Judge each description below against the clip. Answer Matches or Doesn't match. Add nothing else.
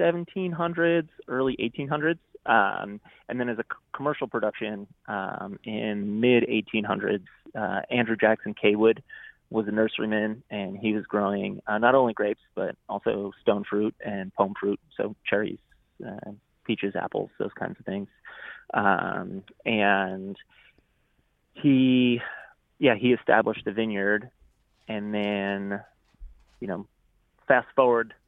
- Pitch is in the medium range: Doesn't match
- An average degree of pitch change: Matches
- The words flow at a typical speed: Doesn't match